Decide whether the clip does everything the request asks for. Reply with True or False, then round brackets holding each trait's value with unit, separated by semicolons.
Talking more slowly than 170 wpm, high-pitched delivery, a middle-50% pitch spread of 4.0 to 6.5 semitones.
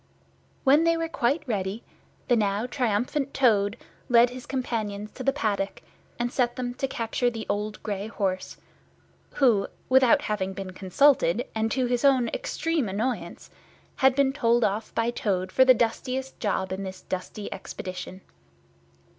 True (155 wpm; 235 Hz; 4.3 semitones)